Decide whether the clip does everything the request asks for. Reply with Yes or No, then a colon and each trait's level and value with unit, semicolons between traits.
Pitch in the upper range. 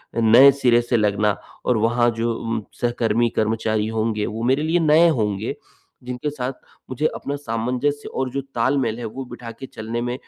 No: low, 120 Hz